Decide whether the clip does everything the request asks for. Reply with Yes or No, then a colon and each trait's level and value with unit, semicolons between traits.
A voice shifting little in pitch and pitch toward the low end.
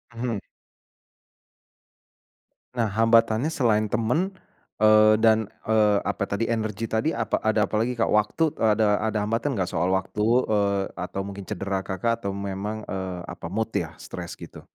Yes: narrow, 2.3 semitones; low, 110 Hz